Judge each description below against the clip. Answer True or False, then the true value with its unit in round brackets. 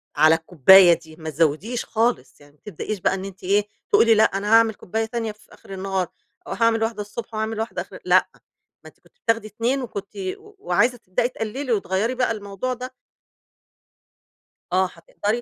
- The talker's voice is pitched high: True (215 Hz)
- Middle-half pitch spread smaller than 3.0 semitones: False (3.5 semitones)